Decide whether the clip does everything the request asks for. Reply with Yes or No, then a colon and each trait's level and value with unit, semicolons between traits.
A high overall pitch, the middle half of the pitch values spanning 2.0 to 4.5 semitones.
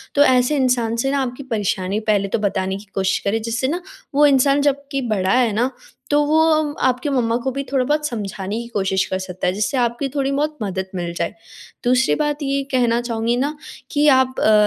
No: high, 245 Hz; average, 4.9 semitones